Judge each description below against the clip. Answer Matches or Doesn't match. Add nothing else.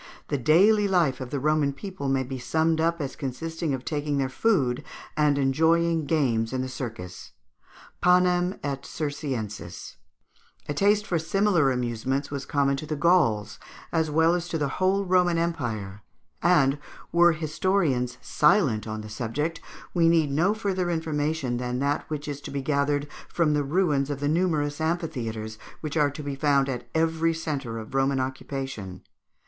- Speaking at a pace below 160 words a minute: Doesn't match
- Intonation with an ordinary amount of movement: Matches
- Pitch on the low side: Doesn't match